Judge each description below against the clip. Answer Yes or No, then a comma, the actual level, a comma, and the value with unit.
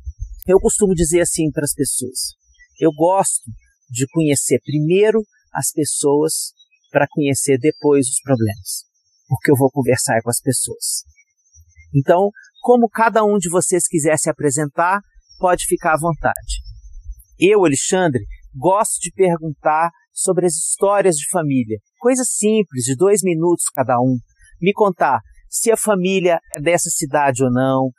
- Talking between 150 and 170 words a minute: No, average, 140 wpm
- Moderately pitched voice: Yes, medium, 155 Hz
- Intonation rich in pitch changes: Yes, wide, 5.9 semitones